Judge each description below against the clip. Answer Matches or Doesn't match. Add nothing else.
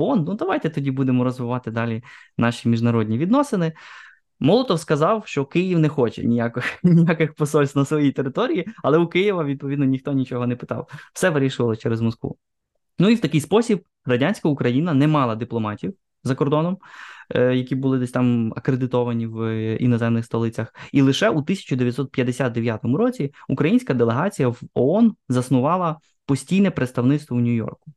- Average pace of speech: Matches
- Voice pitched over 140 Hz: Doesn't match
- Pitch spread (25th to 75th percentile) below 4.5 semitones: Doesn't match